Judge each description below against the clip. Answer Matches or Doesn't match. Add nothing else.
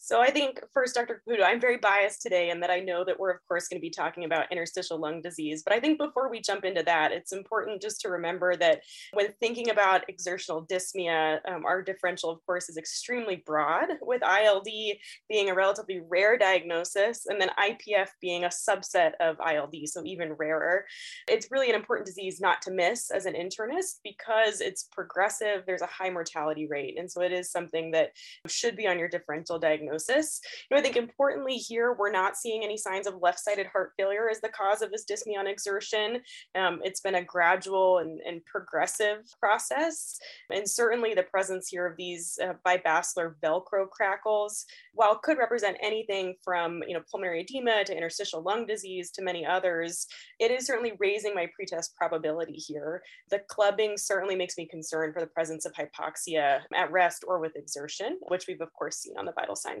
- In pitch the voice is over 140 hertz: Matches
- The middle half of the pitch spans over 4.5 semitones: Doesn't match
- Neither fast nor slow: Matches